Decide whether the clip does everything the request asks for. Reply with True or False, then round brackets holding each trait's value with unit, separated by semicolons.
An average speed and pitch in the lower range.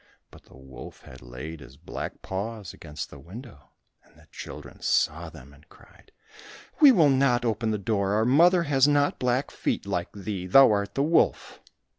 True (180 wpm; 105 Hz)